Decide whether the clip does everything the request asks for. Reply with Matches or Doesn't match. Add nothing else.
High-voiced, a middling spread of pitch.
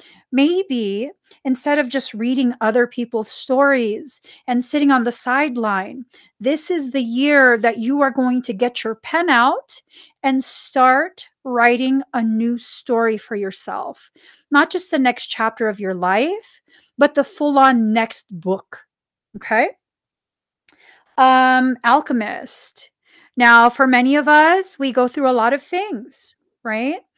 Matches